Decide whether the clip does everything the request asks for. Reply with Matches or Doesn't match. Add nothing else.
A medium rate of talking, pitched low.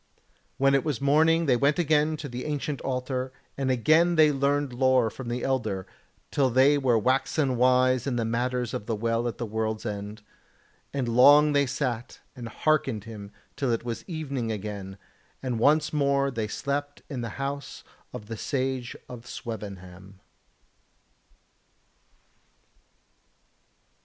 Matches